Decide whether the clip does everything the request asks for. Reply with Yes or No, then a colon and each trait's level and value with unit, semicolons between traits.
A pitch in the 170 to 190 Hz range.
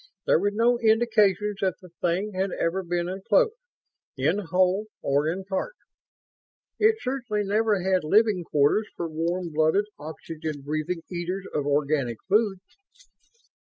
Yes: medium, 185 Hz